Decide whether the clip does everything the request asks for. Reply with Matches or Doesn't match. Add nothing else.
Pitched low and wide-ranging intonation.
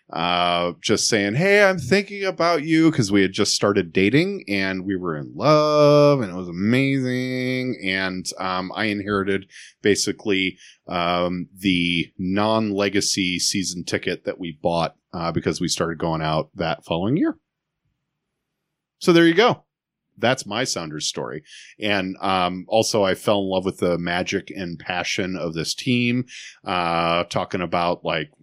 Matches